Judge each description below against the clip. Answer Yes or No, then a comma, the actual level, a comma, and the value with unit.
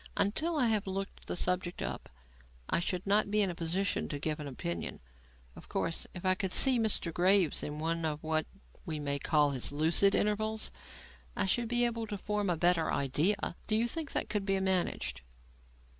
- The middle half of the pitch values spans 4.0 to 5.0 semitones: Yes, average, 4.7 semitones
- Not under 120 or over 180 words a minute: No, average, 195 wpm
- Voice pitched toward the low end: No, medium, 185 Hz